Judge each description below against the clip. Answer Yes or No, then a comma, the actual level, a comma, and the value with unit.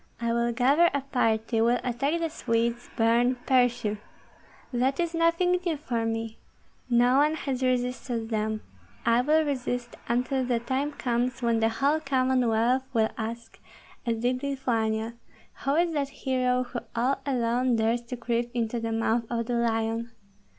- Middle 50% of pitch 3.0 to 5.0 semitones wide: No, narrow, 2.5 semitones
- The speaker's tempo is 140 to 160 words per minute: Yes, average, 155 wpm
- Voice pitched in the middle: No, high, 245 Hz